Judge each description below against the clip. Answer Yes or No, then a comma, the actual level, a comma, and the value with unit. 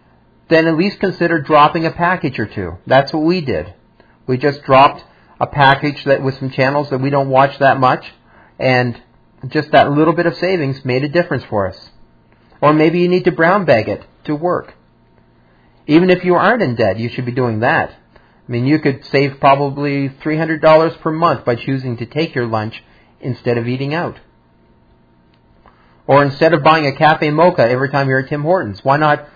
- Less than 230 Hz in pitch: Yes, medium, 140 Hz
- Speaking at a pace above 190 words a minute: Yes, average, 200 wpm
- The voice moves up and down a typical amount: Yes, average, 4.1 semitones